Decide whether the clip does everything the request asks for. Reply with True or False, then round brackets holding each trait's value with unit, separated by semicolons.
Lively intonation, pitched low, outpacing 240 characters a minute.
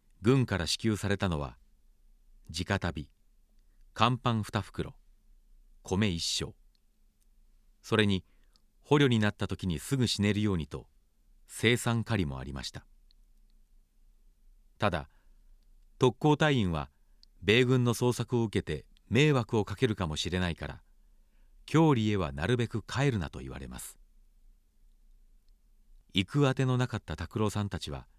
False (7.0 semitones; 100 Hz; 230 characters per minute)